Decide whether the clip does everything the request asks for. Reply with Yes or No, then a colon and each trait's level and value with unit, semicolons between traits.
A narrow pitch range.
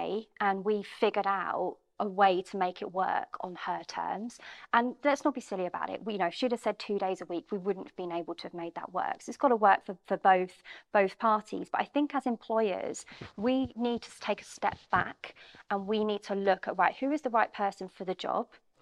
No: average, 3.7 semitones